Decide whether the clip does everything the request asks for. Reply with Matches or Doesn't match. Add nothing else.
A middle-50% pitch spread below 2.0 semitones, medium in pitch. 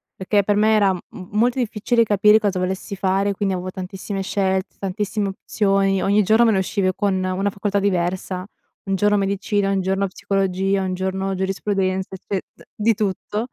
Doesn't match